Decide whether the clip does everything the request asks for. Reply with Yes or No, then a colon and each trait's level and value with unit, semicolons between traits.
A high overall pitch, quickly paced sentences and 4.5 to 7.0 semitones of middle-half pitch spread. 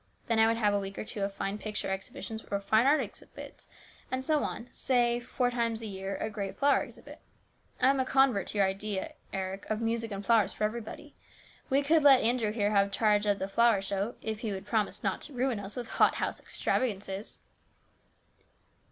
No: high, 220 Hz; fast, 210 wpm; average, 3.4 semitones